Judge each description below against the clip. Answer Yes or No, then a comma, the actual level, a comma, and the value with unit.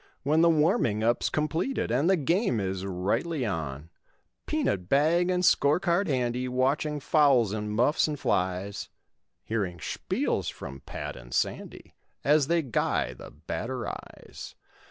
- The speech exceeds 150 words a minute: No, slow, 135 wpm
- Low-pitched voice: Yes, low, 130 Hz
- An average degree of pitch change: No, wide, 7.6 semitones